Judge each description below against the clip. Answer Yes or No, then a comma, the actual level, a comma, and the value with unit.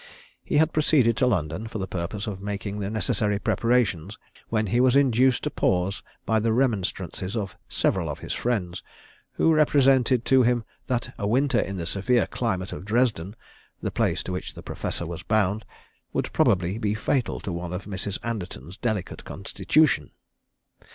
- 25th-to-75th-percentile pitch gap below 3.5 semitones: No, average, 4.6 semitones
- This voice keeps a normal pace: Yes, average, 170 wpm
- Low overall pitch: Yes, low, 105 Hz